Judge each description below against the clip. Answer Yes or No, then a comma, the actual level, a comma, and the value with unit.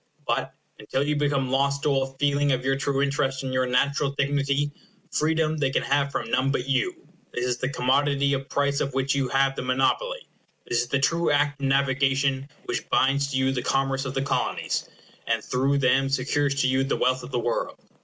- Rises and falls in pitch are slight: Yes, narrow, 1.2 semitones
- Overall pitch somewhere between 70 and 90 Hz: No, low, 135 Hz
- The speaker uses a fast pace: Yes, fast, 210 wpm